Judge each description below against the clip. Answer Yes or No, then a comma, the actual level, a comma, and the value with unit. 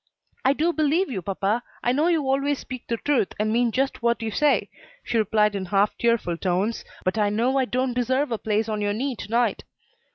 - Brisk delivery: Yes, fast, 220 wpm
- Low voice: No, high, 235 Hz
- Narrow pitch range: No, average, 4.2 semitones